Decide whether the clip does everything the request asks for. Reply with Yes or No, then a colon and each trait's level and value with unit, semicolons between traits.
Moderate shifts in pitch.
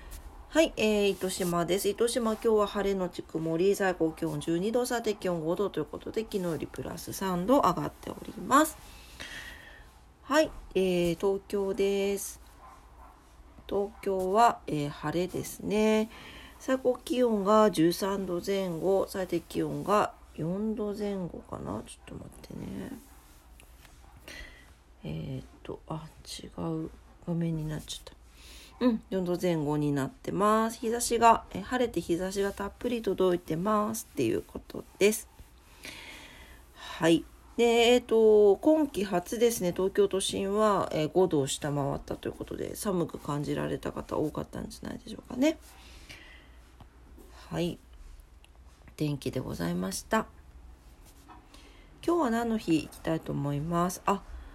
No: wide, 6.4 semitones